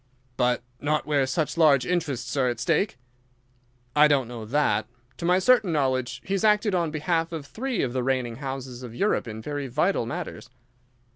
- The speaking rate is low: No, average, 185 wpm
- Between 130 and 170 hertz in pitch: Yes, medium, 140 Hz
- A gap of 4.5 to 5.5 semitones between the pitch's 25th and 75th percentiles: Yes, average, 5.1 semitones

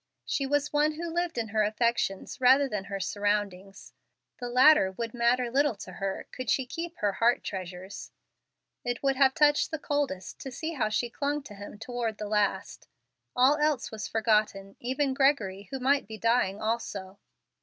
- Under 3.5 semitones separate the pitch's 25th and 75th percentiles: No, average, 5.2 semitones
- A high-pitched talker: Yes, high, 235 Hz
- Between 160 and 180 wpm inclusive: Yes, average, 175 wpm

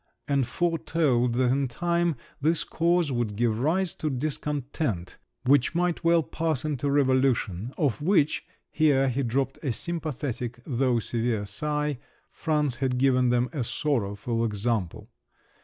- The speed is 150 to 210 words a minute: No, slow, 135 wpm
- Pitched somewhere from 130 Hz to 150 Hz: Yes, low, 135 Hz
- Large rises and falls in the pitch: No, average, 4.1 semitones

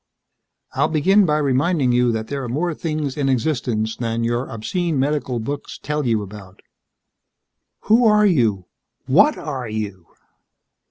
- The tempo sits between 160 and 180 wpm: No, average, 145 wpm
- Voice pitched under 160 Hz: Yes, low, 135 Hz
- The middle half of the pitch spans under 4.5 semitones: No, average, 5.2 semitones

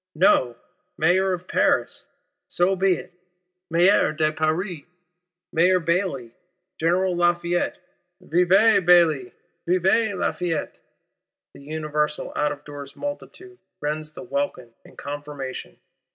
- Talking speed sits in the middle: No, slow, 105 wpm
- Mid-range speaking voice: Yes, medium, 170 Hz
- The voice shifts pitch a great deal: No, average, 3.5 semitones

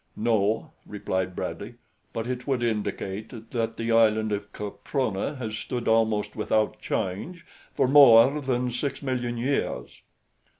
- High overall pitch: No, low, 115 Hz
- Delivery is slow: Yes, slow, 130 wpm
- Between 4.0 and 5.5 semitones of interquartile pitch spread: No, average, 2.9 semitones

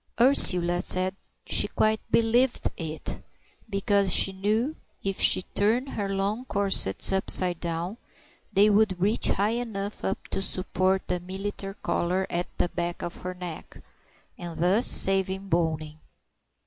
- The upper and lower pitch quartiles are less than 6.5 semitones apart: Yes, average, 2.7 semitones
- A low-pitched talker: No, high, 195 Hz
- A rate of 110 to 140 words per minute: Yes, slow, 135 wpm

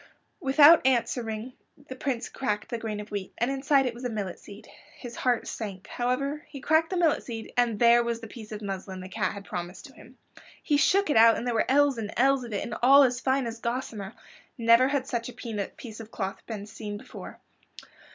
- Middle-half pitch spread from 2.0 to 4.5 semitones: Yes, average, 3.7 semitones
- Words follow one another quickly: Yes, fast, 220 wpm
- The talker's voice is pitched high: Yes, high, 235 Hz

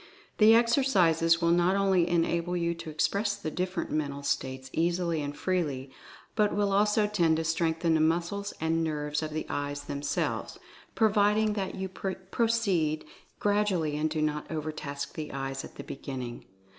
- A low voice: No, medium, 165 Hz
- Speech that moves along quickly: No, average, 160 wpm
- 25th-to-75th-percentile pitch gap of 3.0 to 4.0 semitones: No, average, 4.4 semitones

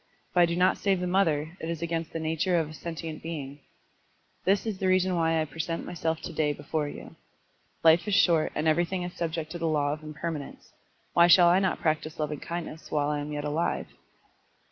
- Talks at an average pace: No, fast, 210 wpm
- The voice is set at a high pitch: No, medium, 165 Hz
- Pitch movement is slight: Yes, narrow, 2.2 semitones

